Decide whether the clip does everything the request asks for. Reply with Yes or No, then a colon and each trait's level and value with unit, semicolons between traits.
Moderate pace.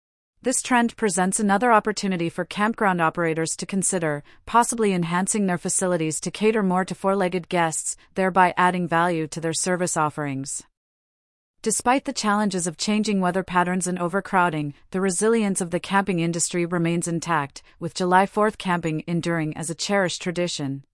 Yes: average, 155 wpm